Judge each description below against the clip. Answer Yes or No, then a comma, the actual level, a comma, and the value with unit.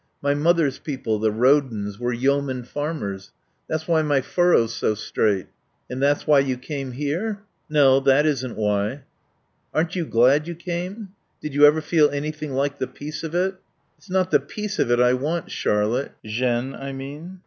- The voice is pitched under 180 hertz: Yes, medium, 140 Hz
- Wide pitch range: No, average, 4.0 semitones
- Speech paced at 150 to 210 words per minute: Yes, average, 175 wpm